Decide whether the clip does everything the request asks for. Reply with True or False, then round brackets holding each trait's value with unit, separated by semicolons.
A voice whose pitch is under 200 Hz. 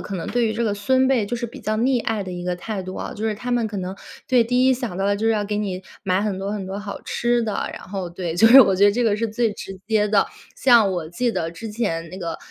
False (210 Hz)